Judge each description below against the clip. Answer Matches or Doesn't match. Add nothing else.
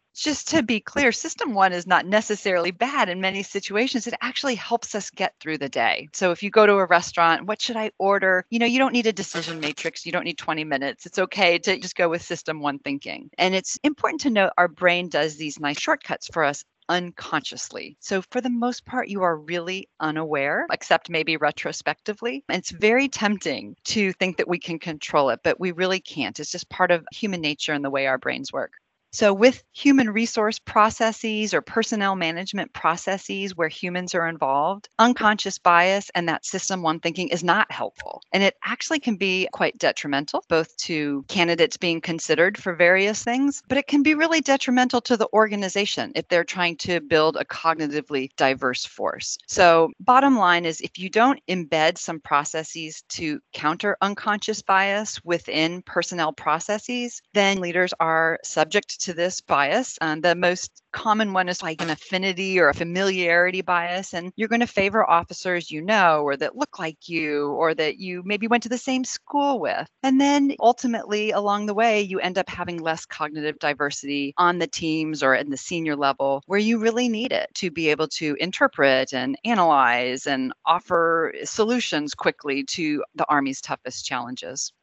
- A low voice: Doesn't match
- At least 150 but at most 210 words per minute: Matches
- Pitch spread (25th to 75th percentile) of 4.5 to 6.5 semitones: Matches